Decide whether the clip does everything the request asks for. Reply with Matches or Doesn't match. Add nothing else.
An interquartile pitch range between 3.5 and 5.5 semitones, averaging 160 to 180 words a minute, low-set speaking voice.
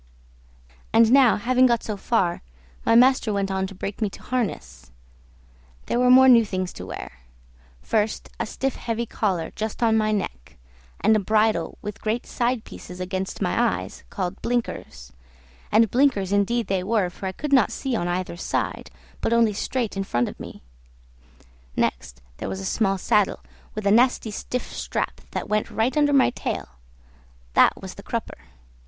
Doesn't match